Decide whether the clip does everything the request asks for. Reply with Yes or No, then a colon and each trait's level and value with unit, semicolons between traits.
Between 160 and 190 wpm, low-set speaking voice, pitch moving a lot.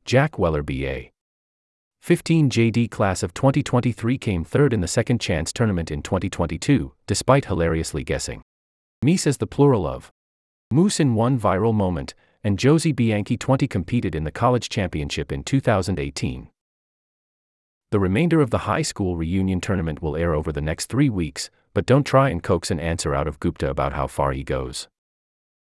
Yes: average, 165 wpm; low, 100 Hz; wide, 7.6 semitones